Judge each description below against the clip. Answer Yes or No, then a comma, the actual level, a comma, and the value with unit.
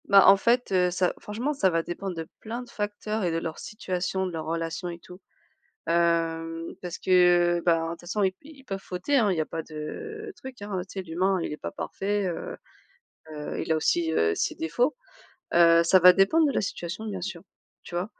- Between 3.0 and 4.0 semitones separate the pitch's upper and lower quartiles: Yes, average, 3.7 semitones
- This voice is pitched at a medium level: Yes, medium, 180 Hz